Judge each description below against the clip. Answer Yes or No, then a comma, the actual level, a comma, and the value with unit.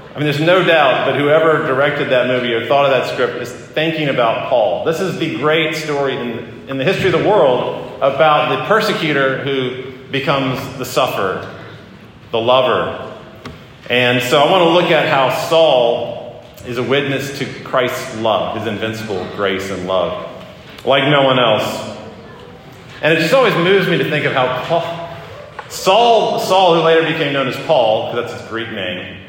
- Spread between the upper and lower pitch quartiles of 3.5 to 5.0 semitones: Yes, average, 4.3 semitones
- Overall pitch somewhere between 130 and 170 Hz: Yes, low, 135 Hz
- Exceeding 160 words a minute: Yes, average, 180 wpm